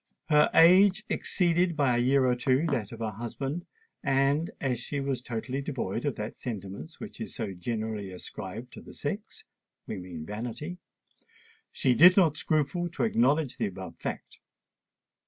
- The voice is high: No, low, 130 Hz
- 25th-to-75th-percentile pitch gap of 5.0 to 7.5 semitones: Yes, wide, 5.6 semitones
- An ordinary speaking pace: Yes, average, 155 wpm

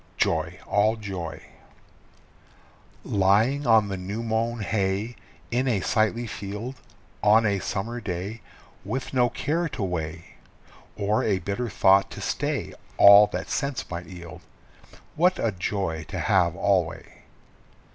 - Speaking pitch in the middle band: No, low, 105 Hz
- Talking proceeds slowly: Yes, slow, 130 wpm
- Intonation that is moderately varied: Yes, average, 3.5 semitones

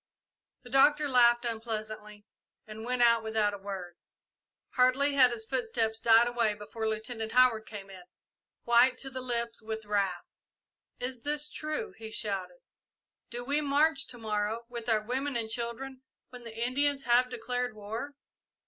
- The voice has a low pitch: No, high, 235 Hz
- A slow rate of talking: No, average, 155 wpm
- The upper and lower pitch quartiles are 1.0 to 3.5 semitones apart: Yes, narrow, 2.6 semitones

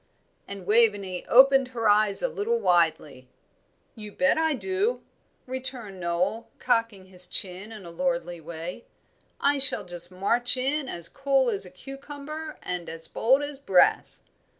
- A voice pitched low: No, high, 225 Hz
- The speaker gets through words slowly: No, average, 150 wpm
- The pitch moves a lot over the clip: Yes, wide, 6.9 semitones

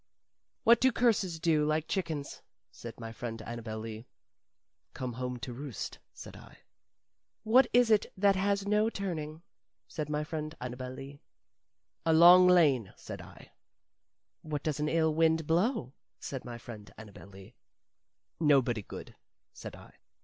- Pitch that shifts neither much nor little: No, wide, 6.6 semitones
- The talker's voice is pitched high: No, medium, 150 Hz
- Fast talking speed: No, average, 145 wpm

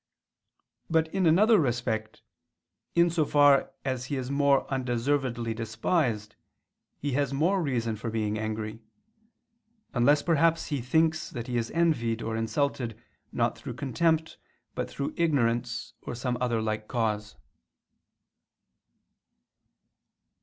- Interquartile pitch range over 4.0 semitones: Yes, average, 5.1 semitones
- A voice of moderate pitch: No, low, 130 Hz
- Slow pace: Yes, slow, 120 wpm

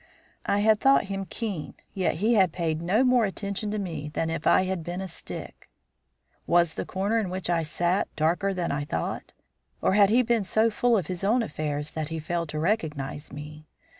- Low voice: No, medium, 180 Hz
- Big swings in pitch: No, average, 4.7 semitones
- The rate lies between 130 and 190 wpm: No, fast, 205 wpm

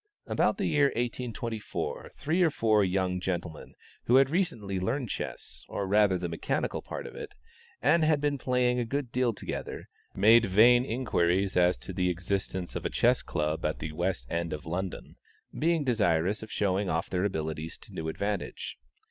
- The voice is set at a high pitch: No, low, 100 Hz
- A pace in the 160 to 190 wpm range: Yes, average, 175 wpm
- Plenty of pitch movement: Yes, wide, 5.8 semitones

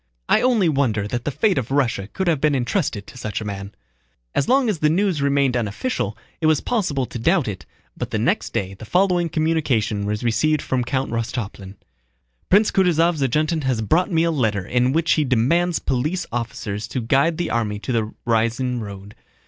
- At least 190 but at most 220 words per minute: Yes, average, 195 wpm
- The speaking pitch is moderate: No, low, 130 Hz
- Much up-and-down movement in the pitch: Yes, wide, 6.7 semitones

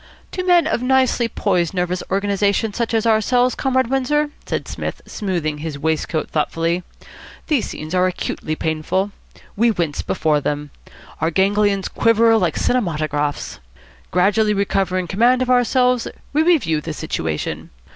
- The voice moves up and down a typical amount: No, wide, 6.9 semitones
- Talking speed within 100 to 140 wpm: Yes, slow, 135 wpm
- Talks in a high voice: Yes, high, 195 Hz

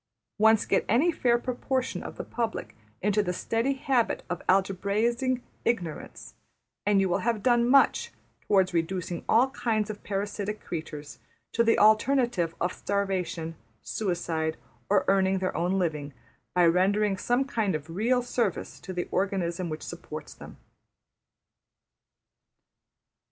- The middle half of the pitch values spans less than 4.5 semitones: No, average, 4.9 semitones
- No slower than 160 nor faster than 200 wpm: No, slow, 135 wpm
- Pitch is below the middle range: No, high, 200 Hz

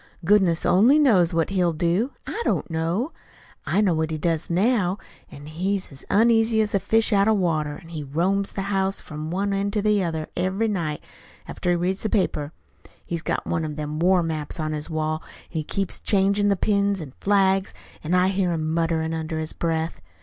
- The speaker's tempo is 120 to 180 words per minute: No, average, 200 wpm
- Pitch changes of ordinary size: Yes, average, 3.9 semitones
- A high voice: No, medium, 180 Hz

